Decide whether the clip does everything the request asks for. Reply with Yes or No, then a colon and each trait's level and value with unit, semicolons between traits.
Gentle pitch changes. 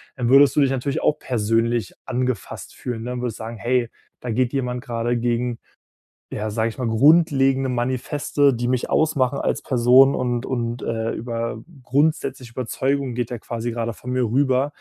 Yes: narrow, 2.3 semitones